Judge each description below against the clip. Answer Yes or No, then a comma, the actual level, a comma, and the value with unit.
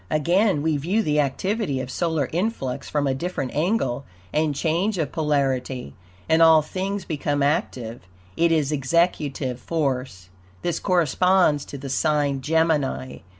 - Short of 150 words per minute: Yes, average, 140 wpm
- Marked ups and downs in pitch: No, average, 3.8 semitones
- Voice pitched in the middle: Yes, medium, 150 Hz